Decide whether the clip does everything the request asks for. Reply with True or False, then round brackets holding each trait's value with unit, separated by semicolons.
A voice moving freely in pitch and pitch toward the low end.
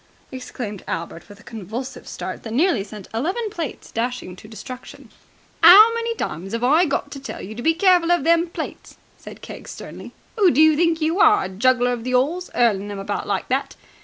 False (7.5 semitones; 255 Hz)